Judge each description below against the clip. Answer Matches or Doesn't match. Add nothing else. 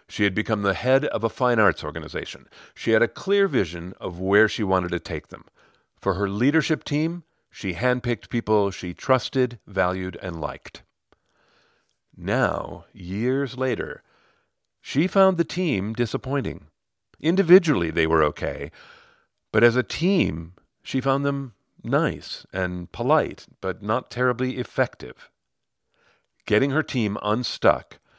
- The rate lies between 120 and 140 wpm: Matches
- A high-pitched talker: Doesn't match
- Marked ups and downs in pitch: Matches